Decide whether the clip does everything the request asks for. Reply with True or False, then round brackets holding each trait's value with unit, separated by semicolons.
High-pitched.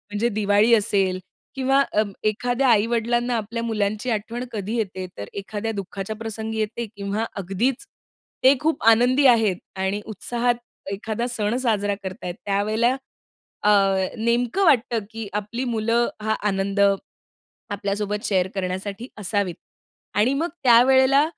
True (220 Hz)